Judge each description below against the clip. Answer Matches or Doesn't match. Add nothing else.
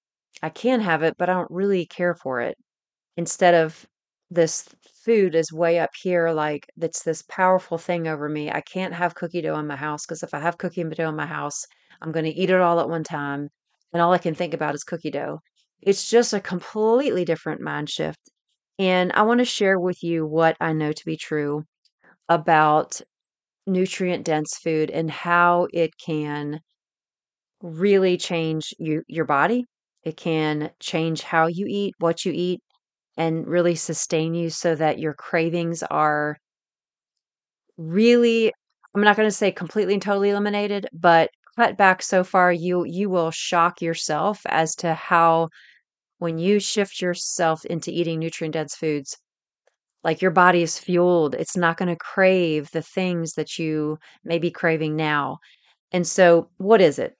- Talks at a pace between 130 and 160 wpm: Doesn't match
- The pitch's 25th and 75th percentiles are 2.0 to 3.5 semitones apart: Matches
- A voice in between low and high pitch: Matches